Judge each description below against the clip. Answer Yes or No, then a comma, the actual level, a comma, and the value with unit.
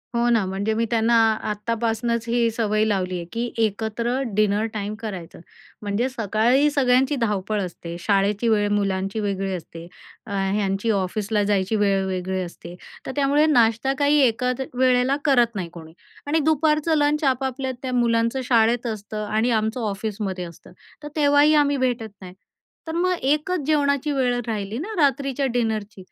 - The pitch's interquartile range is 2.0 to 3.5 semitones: No, average, 4.5 semitones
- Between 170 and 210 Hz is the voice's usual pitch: No, high, 225 Hz